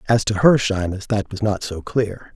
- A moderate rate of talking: No, fast, 230 wpm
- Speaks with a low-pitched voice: Yes, low, 105 Hz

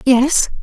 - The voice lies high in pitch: Yes, very high, 265 Hz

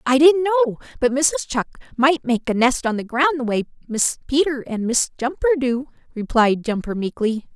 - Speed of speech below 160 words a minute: No, average, 190 wpm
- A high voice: Yes, very high, 260 Hz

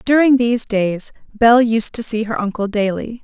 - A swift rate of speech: No, average, 185 wpm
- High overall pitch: Yes, high, 225 Hz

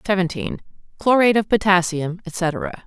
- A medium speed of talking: No, slow, 85 wpm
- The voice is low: No, high, 190 Hz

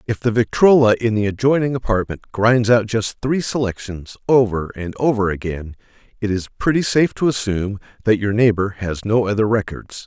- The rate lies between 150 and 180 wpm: Yes, average, 175 wpm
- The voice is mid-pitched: No, low, 110 Hz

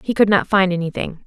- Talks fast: Yes, fast, 240 wpm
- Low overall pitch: No, high, 190 Hz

